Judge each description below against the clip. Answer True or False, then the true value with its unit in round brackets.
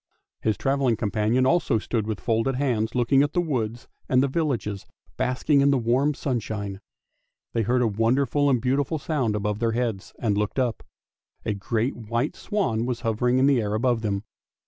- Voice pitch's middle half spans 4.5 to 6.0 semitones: False (3.6 semitones)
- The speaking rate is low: False (185 wpm)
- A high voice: False (120 Hz)